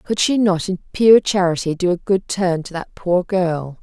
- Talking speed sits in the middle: No, fast, 220 wpm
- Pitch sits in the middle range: Yes, medium, 180 Hz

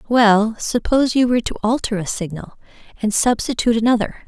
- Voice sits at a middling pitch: No, high, 225 Hz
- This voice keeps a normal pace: Yes, average, 155 wpm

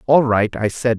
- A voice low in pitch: Yes, low, 120 Hz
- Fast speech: Yes, fast, 245 wpm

